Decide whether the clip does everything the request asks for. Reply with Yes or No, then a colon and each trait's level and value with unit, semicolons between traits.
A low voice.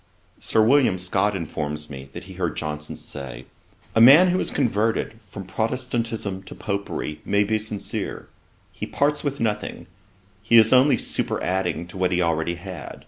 Yes: low, 100 Hz